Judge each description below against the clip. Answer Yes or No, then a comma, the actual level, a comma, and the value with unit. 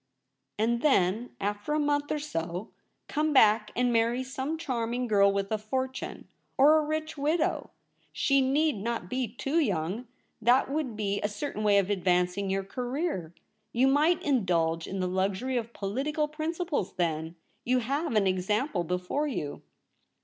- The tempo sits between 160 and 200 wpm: Yes, average, 165 wpm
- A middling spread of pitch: No, wide, 6.5 semitones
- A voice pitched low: No, high, 235 Hz